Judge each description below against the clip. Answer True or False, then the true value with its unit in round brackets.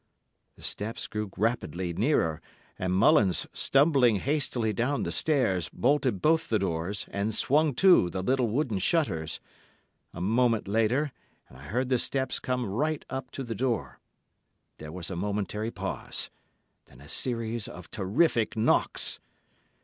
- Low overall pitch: True (115 Hz)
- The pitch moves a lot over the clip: True (5.7 semitones)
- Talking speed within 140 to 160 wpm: True (145 wpm)